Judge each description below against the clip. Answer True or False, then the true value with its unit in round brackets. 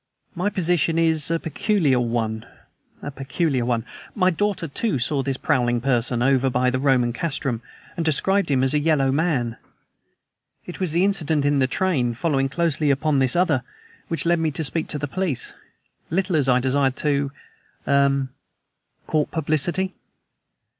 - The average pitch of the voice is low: False (145 Hz)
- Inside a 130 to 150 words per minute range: False (160 wpm)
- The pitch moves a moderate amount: True (4.1 semitones)